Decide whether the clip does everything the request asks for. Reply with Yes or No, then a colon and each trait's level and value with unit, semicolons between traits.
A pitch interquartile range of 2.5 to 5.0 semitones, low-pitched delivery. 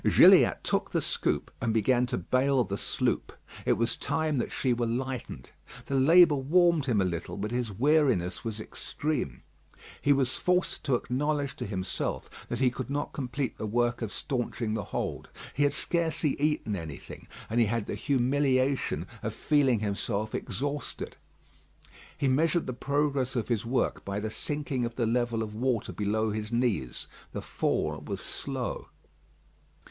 Yes: average, 4.4 semitones; low, 125 Hz